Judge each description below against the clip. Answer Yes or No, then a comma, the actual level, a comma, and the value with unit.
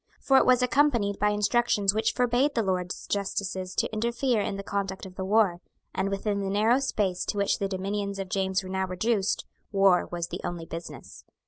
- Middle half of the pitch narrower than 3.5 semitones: Yes, average, 2.7 semitones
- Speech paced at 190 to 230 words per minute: Yes, average, 200 wpm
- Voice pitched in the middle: No, high, 200 Hz